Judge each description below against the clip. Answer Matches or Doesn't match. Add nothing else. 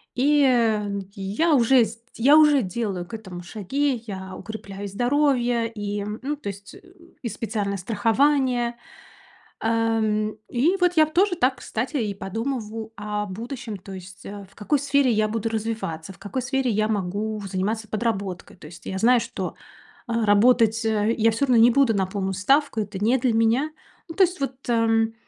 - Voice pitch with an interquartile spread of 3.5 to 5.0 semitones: Matches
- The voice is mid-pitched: Doesn't match